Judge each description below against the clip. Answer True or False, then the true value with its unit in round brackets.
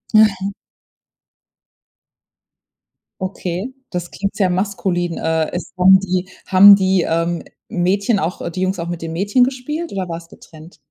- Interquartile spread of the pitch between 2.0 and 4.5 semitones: True (2.4 semitones)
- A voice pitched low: False (185 Hz)